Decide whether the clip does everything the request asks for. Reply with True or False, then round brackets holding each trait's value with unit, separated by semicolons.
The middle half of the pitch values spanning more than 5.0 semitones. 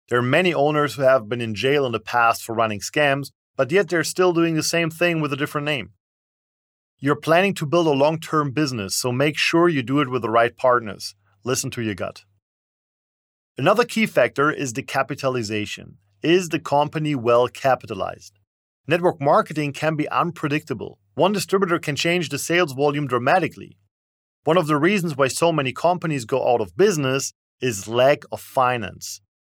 True (5.4 semitones)